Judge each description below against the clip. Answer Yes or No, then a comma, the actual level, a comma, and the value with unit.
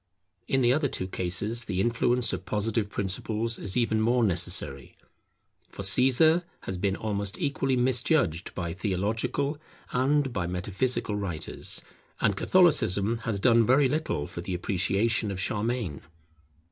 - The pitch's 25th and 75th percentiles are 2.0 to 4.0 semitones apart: No, average, 4.8 semitones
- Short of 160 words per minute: Yes, slow, 135 wpm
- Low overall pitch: Yes, low, 110 Hz